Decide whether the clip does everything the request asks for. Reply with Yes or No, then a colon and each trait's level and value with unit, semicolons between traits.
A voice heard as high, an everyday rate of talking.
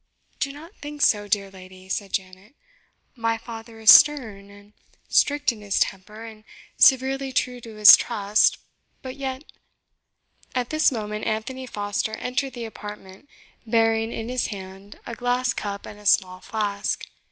Yes: high, 225 Hz; average, 155 wpm